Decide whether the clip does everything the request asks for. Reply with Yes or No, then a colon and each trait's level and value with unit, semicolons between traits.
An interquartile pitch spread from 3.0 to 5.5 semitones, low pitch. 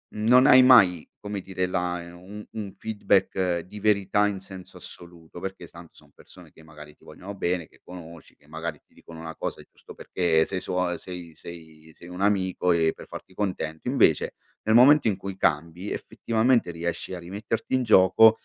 Yes: average, 3.3 semitones; very low, 90 Hz